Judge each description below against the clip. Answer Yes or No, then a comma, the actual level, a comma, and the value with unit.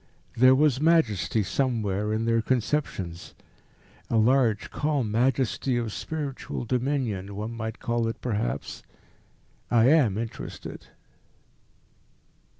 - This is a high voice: No, low, 115 Hz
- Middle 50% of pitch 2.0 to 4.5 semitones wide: Yes, average, 3.5 semitones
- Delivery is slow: Yes, slow, 105 wpm